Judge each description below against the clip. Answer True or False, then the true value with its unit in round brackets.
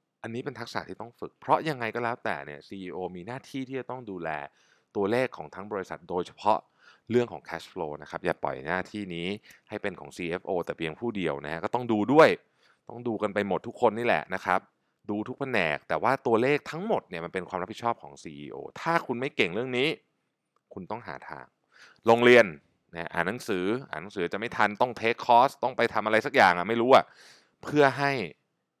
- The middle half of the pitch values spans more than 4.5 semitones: True (4.9 semitones)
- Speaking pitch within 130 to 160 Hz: False (110 Hz)